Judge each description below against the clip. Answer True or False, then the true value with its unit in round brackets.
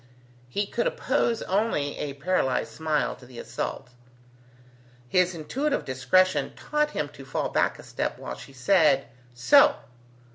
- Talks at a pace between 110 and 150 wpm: True (140 wpm)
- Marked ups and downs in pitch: True (7.2 semitones)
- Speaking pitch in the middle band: True (160 Hz)